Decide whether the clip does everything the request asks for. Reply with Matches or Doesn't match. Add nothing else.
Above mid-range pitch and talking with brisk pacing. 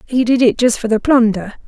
Matches